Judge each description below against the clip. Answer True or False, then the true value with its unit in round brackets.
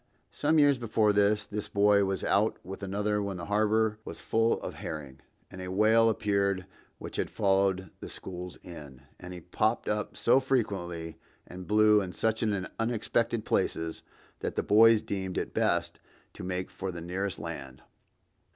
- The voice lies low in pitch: True (100 Hz)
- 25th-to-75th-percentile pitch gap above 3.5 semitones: False (3.0 semitones)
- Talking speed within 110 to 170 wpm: True (165 wpm)